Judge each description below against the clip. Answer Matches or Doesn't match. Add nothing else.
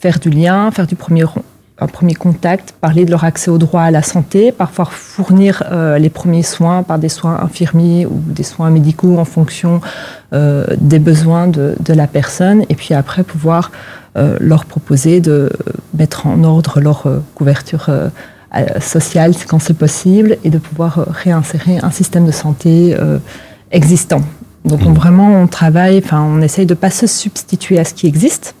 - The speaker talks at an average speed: Matches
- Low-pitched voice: Doesn't match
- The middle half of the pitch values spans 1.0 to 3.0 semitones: Matches